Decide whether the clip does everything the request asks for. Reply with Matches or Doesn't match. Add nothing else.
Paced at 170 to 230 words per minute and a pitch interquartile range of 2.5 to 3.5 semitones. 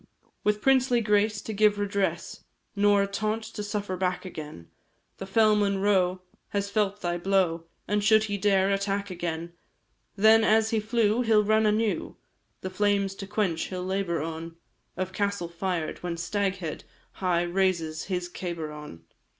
Doesn't match